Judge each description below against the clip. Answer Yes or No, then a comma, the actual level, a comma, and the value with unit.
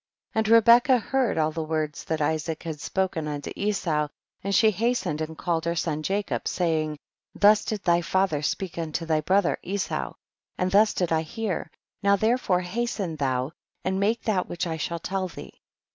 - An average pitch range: Yes, average, 4.3 semitones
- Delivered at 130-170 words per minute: No, average, 180 wpm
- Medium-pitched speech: Yes, medium, 180 Hz